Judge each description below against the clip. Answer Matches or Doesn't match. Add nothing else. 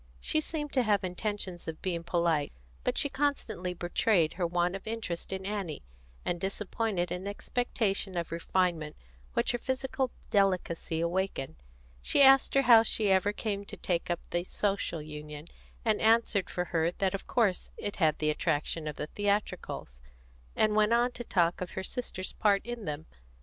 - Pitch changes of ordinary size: Matches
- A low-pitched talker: Doesn't match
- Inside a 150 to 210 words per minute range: Matches